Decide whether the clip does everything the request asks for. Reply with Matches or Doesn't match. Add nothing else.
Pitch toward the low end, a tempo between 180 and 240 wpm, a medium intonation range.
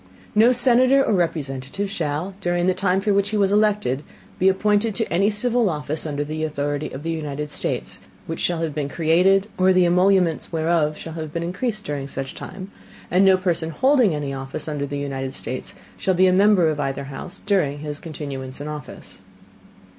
Doesn't match